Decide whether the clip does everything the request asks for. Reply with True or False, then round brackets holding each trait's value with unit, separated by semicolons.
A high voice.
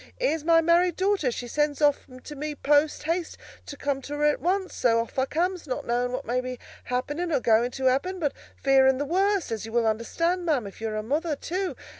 True (290 Hz)